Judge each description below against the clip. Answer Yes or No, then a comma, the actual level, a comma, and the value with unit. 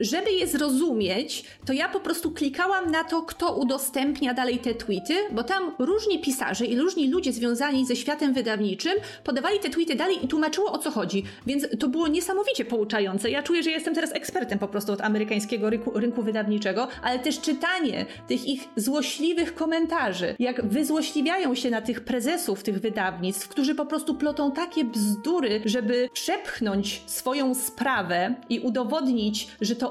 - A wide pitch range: Yes, wide, 6.0 semitones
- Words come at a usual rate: No, fast, 165 wpm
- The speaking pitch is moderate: No, very high, 270 Hz